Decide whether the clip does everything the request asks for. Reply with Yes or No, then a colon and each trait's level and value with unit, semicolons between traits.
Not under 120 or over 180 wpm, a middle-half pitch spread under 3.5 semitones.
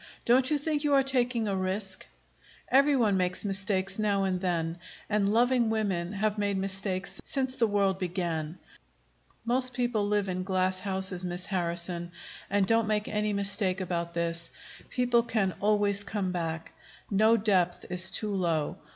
Yes: average, 160 wpm; average, 3.0 semitones